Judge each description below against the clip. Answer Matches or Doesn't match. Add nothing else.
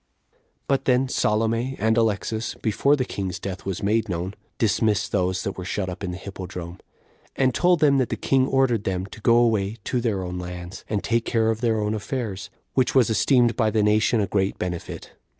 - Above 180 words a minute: Matches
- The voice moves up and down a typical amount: Matches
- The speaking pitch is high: Doesn't match